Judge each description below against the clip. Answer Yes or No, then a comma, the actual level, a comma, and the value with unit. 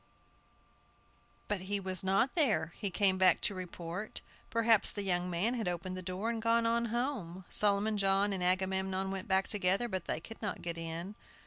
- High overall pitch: Yes, high, 195 Hz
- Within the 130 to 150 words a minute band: No, average, 185 wpm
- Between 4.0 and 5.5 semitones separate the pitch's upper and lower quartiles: No, average, 2.8 semitones